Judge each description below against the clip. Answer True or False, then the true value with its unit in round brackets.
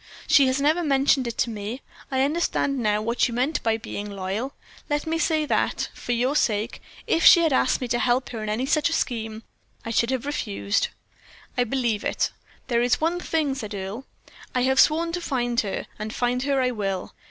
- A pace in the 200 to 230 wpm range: True (205 wpm)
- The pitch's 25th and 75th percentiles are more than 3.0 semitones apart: True (4.2 semitones)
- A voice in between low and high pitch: False (250 Hz)